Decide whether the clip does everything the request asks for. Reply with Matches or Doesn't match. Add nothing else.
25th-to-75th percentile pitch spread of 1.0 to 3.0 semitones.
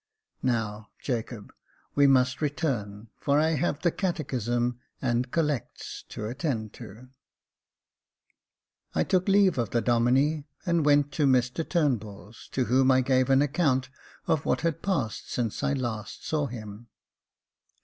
Doesn't match